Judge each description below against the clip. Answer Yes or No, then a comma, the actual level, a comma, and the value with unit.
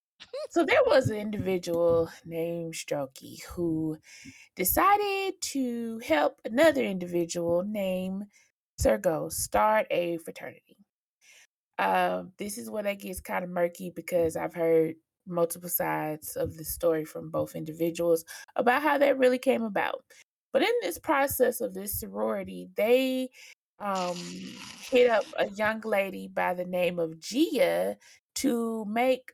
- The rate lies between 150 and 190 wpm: No, slow, 135 wpm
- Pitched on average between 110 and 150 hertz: No, high, 190 Hz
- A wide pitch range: Yes, wide, 7.2 semitones